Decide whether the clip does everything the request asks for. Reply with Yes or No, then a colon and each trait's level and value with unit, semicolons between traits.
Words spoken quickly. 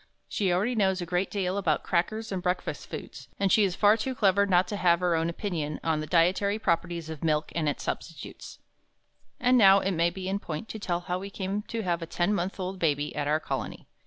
Yes: fast, 230 wpm